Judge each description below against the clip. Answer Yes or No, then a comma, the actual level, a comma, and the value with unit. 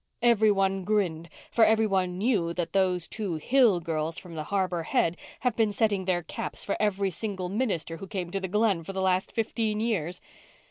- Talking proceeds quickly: No, average, 195 wpm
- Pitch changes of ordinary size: Yes, average, 3.5 semitones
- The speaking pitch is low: No, high, 190 Hz